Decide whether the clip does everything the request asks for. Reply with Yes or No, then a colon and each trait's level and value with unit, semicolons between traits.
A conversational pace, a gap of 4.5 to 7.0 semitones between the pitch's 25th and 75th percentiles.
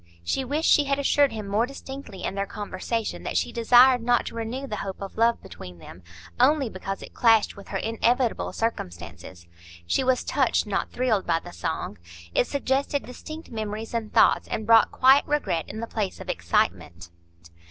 Yes: average, 185 wpm; average, 4.8 semitones